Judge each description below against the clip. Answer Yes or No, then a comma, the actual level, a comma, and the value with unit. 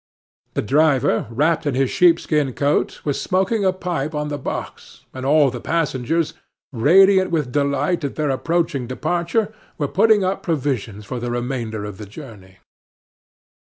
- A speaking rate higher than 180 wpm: No, average, 155 wpm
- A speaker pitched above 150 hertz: No, medium, 145 Hz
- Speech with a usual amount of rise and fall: Yes, average, 4.9 semitones